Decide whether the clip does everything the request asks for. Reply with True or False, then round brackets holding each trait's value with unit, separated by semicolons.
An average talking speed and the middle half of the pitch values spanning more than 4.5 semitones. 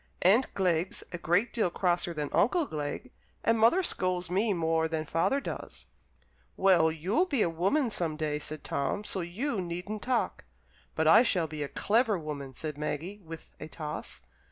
True (175 wpm; 5.1 semitones)